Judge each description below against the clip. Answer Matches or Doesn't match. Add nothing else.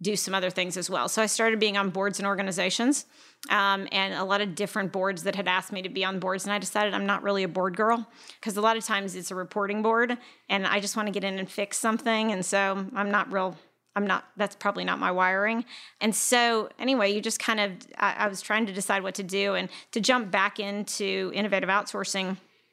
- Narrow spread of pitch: Matches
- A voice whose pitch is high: Matches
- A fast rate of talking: Matches